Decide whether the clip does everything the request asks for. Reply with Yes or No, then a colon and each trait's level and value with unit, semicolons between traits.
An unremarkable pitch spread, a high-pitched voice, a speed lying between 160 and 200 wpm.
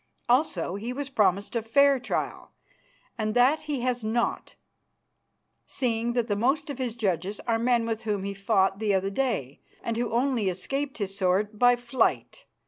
Yes: average, 3.8 semitones; high, 230 Hz; average, 170 wpm